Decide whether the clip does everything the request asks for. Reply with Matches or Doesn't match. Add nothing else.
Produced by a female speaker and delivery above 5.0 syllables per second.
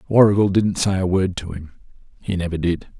Doesn't match